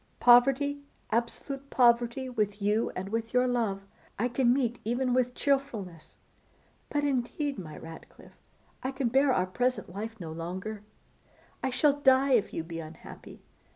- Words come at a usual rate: Yes, average, 150 wpm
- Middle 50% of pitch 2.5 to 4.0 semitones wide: No, average, 4.6 semitones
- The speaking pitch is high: Yes, high, 240 Hz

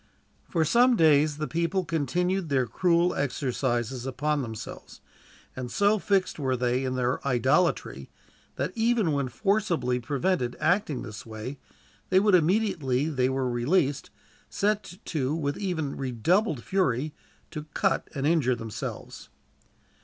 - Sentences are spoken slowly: Yes, slow, 130 wpm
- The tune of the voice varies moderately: No, wide, 6.0 semitones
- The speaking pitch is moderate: Yes, medium, 145 Hz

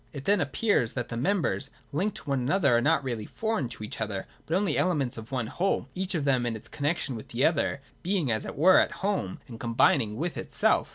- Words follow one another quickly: Yes, fast, 230 wpm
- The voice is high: No, medium, 140 Hz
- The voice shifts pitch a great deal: Yes, wide, 7.3 semitones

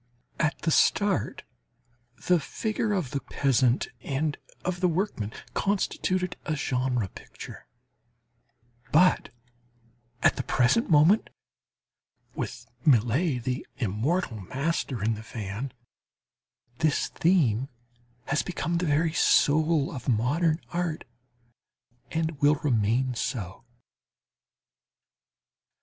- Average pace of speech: No, slow, 100 wpm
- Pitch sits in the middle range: Yes, medium, 145 Hz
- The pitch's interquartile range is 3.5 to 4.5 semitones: No, wide, 5.6 semitones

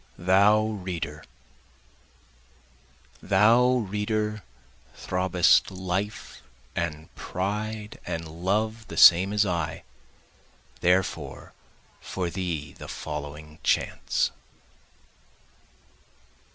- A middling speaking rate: No, slow, 75 wpm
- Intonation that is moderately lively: Yes, average, 4.0 semitones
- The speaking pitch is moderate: No, very low, 95 Hz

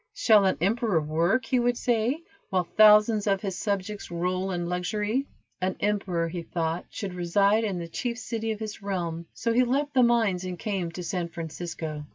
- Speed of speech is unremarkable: Yes, average, 190 wpm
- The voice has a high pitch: Yes, high, 195 Hz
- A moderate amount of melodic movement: Yes, average, 4.2 semitones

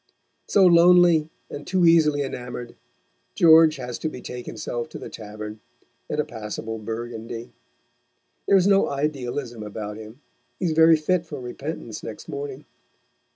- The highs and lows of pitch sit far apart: Yes, wide, 6.0 semitones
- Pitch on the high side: No, medium, 140 Hz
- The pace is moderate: Yes, average, 145 wpm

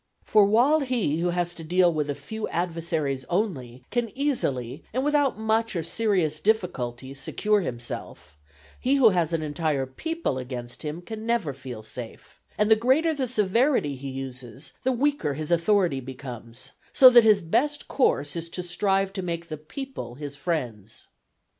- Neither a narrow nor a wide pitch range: No, wide, 8.2 semitones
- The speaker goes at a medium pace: Yes, average, 165 wpm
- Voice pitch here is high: No, medium, 170 Hz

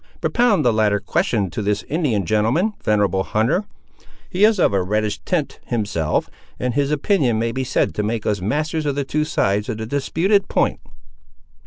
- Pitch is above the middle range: No, low, 115 Hz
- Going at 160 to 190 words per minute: Yes, average, 180 wpm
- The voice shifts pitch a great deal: Yes, wide, 6.5 semitones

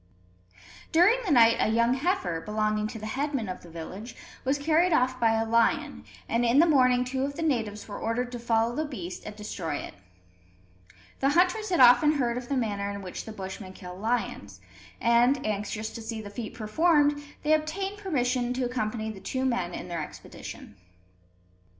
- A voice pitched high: Yes, high, 240 Hz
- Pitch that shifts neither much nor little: Yes, average, 4.8 semitones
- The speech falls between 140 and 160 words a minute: No, average, 185 wpm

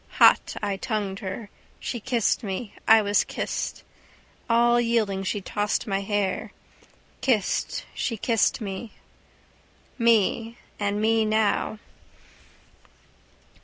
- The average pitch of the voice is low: No, high, 215 Hz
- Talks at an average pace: No, slow, 105 wpm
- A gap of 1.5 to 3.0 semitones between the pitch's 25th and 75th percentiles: Yes, narrow, 2.4 semitones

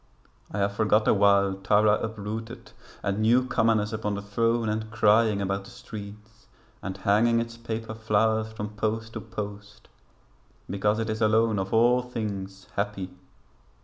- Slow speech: No, average, 145 wpm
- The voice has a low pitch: Yes, low, 110 Hz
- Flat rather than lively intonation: Yes, narrow, 1.8 semitones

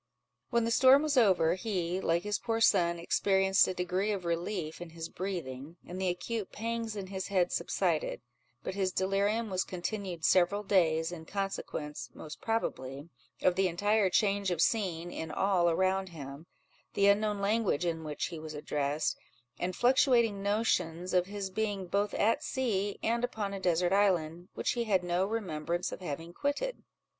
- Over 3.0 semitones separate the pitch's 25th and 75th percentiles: Yes, average, 3.5 semitones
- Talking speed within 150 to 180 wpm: Yes, average, 170 wpm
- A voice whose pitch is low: No, high, 190 Hz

